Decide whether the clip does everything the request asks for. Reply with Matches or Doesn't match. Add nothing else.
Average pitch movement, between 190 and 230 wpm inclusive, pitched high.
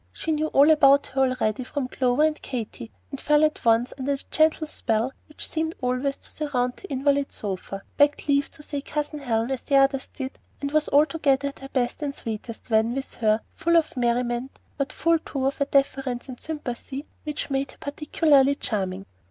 Matches